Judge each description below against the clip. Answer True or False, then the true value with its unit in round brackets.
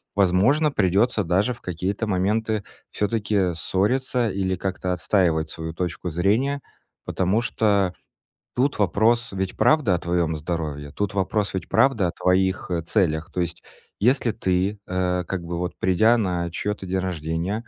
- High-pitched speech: False (95 Hz)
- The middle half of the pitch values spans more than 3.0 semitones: True (3.4 semitones)